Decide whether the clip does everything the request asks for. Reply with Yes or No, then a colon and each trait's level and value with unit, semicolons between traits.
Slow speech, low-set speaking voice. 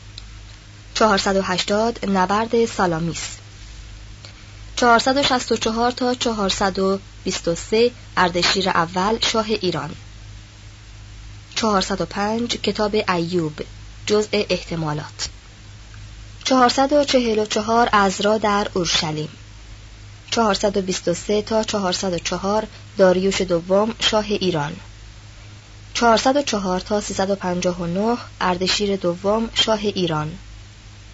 No: slow, 65 wpm; medium, 185 Hz